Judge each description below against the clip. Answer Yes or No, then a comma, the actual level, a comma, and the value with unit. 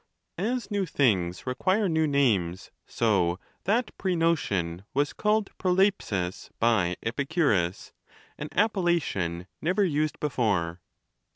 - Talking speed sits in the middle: No, slow, 100 wpm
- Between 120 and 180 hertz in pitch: Yes, medium, 140 Hz